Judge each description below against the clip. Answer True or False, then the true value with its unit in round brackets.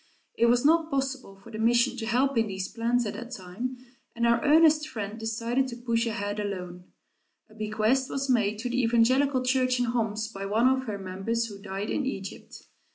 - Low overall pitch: False (230 Hz)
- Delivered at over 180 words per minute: True (200 wpm)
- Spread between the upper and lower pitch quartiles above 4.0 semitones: False (3.3 semitones)